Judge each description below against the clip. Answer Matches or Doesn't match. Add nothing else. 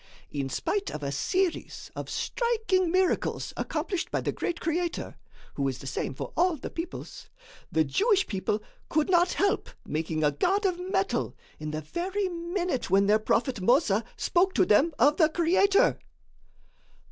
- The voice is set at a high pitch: Matches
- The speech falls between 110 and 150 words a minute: Doesn't match